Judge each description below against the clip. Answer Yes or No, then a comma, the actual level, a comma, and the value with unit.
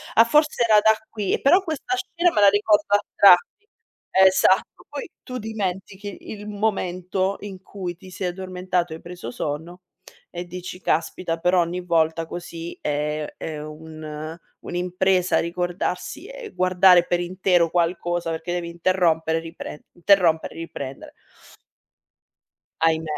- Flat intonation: No, average, 3.1 semitones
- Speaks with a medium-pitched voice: Yes, medium, 180 Hz